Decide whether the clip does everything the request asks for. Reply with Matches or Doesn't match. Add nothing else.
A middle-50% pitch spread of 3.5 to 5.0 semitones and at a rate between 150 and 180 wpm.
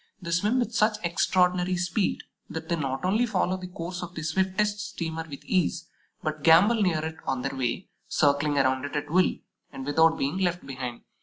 Doesn't match